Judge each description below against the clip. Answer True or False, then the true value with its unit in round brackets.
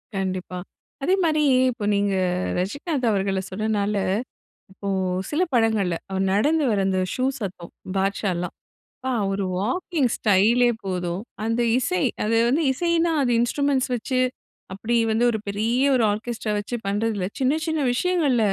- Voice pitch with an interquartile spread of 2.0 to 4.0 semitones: False (4.8 semitones)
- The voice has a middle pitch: False (220 Hz)